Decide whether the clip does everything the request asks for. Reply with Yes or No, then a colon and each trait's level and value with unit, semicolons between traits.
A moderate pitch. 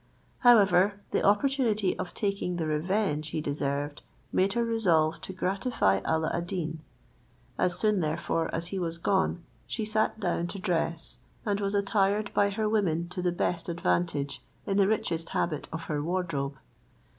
Yes: medium, 180 Hz